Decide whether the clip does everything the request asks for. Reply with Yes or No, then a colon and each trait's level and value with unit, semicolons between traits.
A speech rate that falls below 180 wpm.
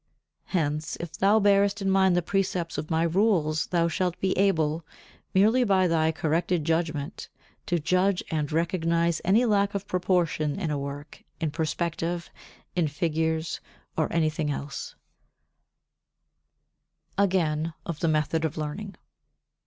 Yes: average, 140 wpm